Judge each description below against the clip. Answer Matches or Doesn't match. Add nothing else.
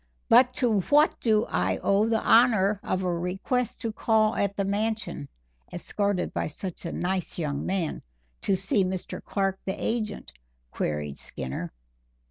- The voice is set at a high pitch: Matches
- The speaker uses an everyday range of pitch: Matches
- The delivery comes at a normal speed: Matches